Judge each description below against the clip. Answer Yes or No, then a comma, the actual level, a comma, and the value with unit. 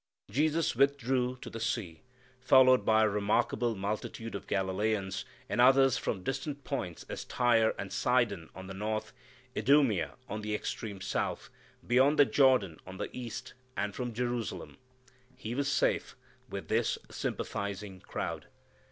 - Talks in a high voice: No, low, 115 Hz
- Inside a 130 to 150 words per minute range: Yes, average, 145 wpm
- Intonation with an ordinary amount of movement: Yes, average, 4.2 semitones